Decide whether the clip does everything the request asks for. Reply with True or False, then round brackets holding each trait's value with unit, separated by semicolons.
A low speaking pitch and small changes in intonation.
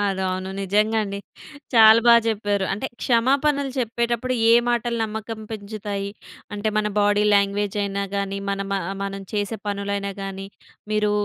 False (205 Hz; 2.3 semitones)